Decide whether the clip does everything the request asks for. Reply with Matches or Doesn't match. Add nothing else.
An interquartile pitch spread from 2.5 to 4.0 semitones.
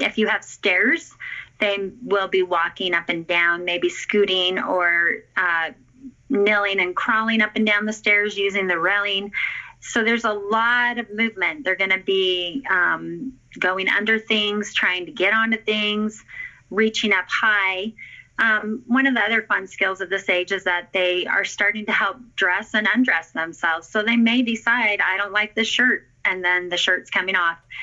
Matches